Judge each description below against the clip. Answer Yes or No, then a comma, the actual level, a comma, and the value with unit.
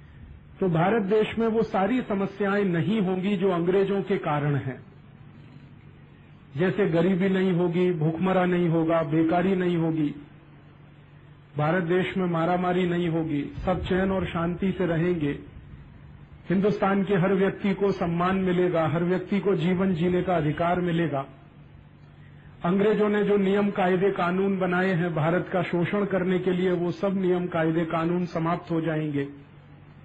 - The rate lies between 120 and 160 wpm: Yes, average, 145 wpm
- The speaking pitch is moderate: Yes, medium, 180 Hz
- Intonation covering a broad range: No, average, 2.7 semitones